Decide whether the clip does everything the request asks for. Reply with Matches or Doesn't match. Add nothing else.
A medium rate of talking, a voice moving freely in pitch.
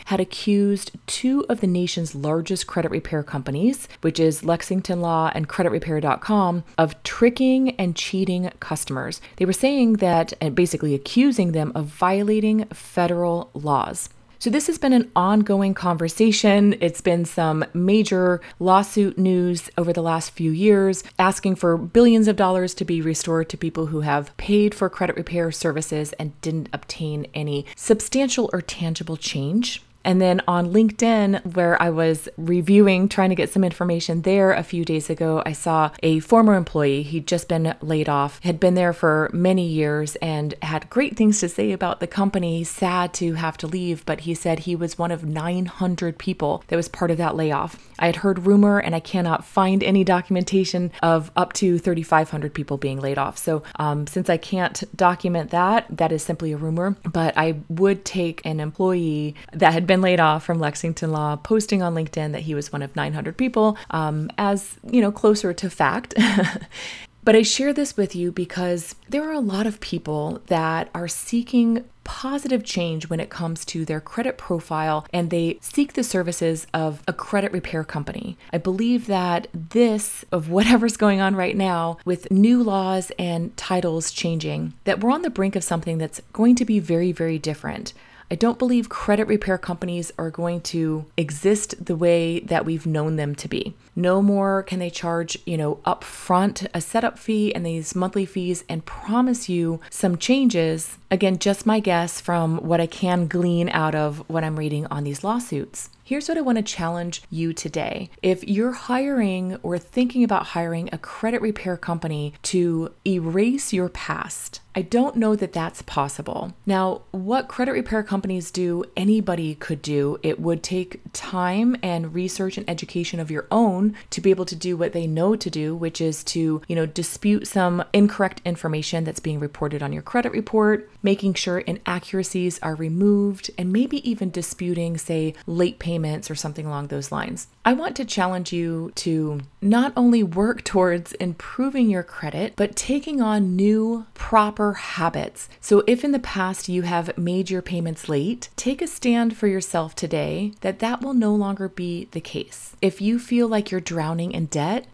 Doesn't match